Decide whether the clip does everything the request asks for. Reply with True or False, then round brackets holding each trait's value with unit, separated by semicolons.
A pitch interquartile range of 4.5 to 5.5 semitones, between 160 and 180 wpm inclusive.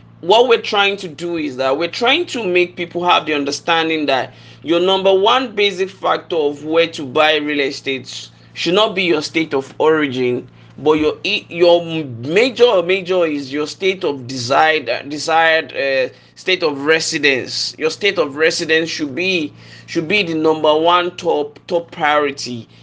False (3.7 semitones; 170 wpm)